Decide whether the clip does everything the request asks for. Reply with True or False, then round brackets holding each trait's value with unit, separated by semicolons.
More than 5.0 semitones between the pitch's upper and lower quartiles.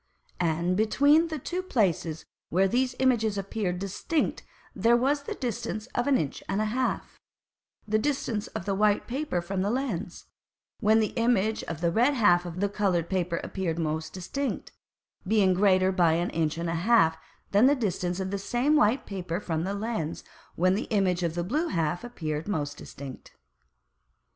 True (5.4 semitones)